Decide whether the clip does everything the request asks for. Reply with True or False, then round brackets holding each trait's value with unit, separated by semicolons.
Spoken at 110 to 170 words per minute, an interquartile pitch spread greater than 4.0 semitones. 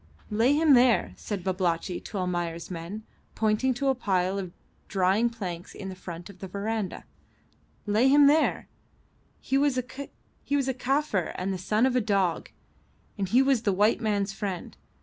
True (160 wpm; 5.4 semitones)